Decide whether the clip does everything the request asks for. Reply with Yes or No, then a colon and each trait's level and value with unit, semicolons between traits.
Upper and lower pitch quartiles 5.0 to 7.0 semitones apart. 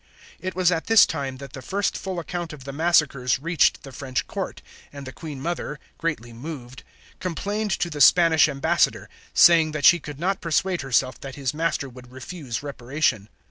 No: average, 4.4 semitones